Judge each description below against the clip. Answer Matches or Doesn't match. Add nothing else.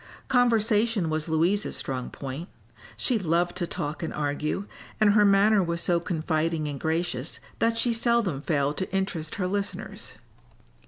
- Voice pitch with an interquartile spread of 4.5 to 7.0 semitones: Matches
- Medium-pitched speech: Matches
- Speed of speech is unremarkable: Matches